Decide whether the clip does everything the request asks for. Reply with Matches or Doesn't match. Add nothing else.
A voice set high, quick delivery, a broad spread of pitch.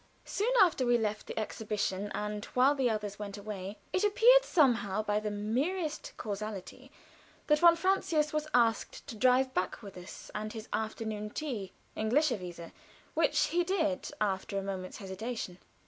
Doesn't match